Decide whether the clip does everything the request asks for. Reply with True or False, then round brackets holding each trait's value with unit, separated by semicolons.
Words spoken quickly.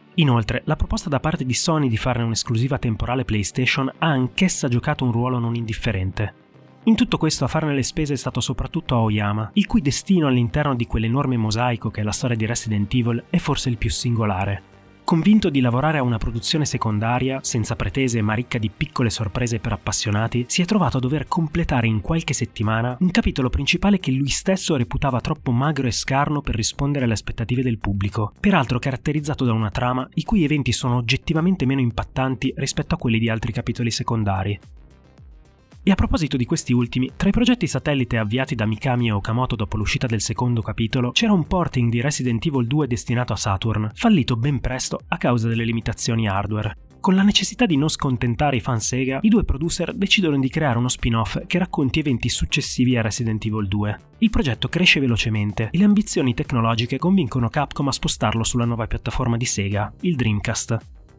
True (190 wpm)